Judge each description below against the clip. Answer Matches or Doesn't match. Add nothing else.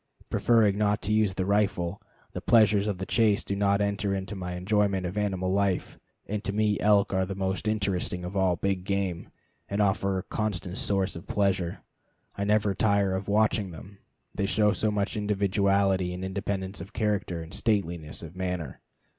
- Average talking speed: Matches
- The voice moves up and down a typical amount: Doesn't match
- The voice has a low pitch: Matches